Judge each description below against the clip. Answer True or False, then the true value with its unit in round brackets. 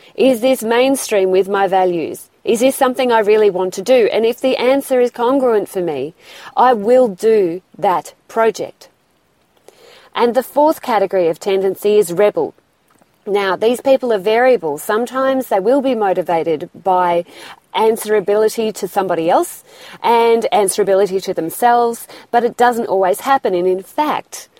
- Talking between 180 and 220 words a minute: False (150 wpm)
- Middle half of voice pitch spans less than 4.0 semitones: False (4.8 semitones)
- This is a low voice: False (220 Hz)